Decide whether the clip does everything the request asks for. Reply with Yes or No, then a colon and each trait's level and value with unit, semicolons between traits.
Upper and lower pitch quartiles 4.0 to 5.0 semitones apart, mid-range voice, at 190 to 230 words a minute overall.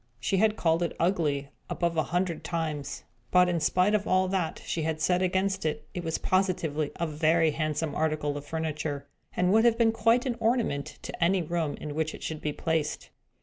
No: average, 3.3 semitones; medium, 165 Hz; average, 200 wpm